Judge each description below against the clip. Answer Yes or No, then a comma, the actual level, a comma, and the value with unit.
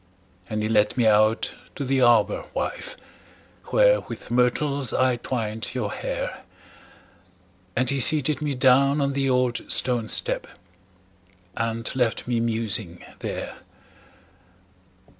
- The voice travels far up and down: No, average, 3.3 semitones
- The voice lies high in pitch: No, low, 125 Hz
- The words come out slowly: Yes, slow, 120 wpm